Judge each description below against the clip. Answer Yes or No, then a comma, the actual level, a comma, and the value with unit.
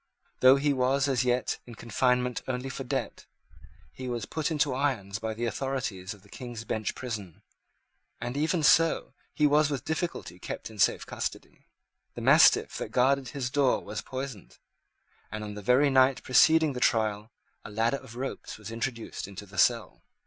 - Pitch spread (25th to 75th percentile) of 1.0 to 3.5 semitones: No, average, 3.9 semitones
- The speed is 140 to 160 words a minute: No, average, 175 wpm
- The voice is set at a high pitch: No, low, 125 Hz